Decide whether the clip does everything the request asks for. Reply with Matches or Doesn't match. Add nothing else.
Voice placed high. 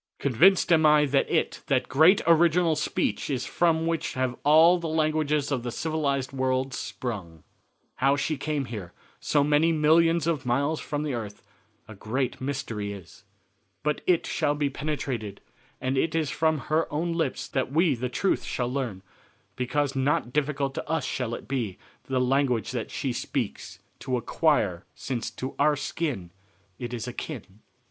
Doesn't match